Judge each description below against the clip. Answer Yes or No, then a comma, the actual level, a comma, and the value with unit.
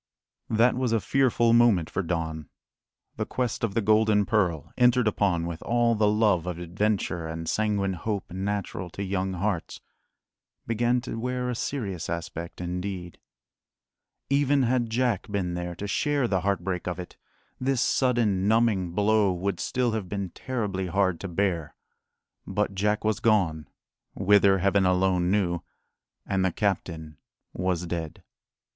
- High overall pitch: No, low, 100 Hz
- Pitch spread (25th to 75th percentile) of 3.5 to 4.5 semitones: Yes, average, 4.1 semitones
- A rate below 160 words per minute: Yes, average, 150 wpm